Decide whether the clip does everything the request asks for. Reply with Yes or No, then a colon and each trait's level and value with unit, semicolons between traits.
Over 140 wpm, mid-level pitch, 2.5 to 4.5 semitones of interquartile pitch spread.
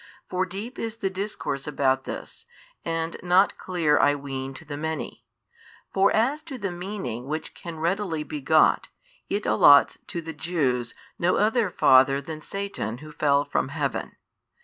No: average, 165 wpm; medium, 160 Hz; average, 5.3 semitones